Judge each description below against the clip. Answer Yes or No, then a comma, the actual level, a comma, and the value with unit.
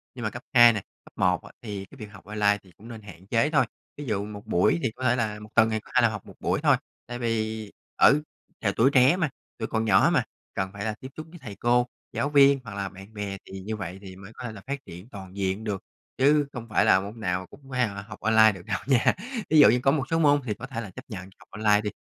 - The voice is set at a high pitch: No, low, 110 Hz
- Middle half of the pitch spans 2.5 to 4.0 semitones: Yes, average, 3.7 semitones